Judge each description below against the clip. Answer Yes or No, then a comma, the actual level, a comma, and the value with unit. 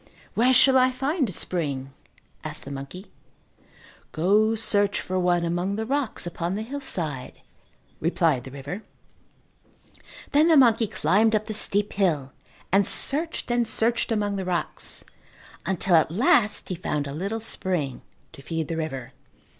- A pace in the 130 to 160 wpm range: Yes, average, 150 wpm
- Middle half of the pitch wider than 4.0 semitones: Yes, wide, 5.6 semitones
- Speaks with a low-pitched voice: No, high, 190 Hz